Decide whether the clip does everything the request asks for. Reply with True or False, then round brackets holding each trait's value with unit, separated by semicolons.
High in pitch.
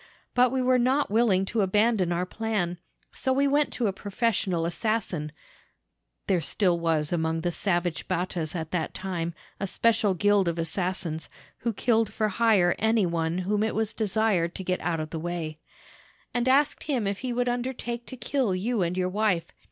True (195 Hz)